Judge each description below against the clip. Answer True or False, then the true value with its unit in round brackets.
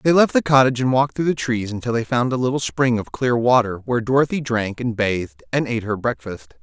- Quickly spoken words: True (245 wpm)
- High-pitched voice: False (120 Hz)